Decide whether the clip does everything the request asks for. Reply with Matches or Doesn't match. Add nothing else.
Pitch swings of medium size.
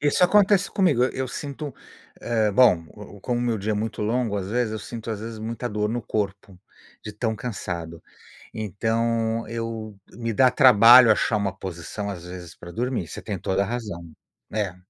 Matches